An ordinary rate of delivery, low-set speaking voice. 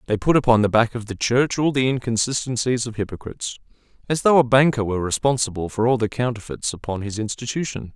Yes: average, 190 wpm; low, 120 Hz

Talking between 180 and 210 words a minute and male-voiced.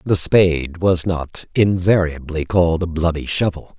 No: average, 145 wpm; male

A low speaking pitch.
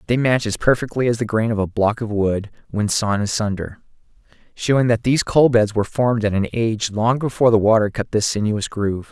Yes: low, 110 Hz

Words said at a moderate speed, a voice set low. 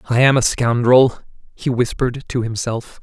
Yes: average, 160 wpm; low, 120 Hz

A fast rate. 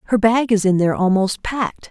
Yes: fast, 220 wpm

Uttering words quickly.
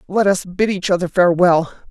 No: average, 190 wpm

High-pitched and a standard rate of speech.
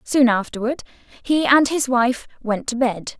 Yes: very high, 250 Hz; average, 170 wpm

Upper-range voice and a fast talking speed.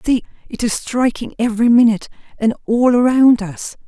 No: high, 235 Hz; average, 155 wpm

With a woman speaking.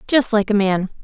Yes: female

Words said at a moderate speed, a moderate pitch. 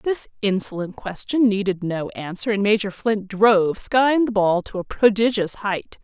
No: average, 170 wpm; high, 205 Hz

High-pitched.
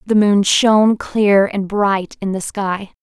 Yes: high, 200 Hz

